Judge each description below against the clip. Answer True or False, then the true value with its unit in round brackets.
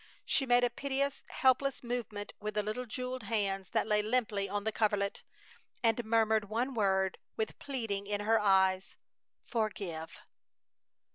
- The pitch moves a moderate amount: True (3.3 semitones)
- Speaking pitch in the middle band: False (215 Hz)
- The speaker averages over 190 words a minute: False (145 wpm)